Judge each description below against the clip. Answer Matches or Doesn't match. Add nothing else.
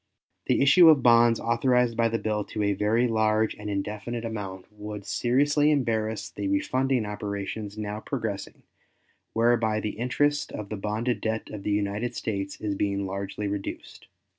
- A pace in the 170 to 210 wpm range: Doesn't match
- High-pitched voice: Doesn't match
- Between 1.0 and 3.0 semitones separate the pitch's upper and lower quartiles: Matches